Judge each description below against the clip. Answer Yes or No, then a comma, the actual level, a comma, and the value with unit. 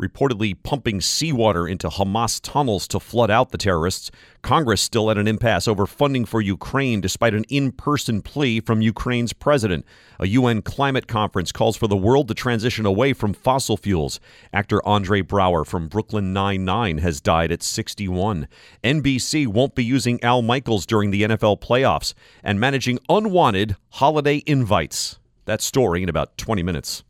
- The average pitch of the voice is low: Yes, low, 110 Hz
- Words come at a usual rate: Yes, average, 160 wpm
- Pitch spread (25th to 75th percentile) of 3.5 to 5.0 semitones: Yes, average, 4.5 semitones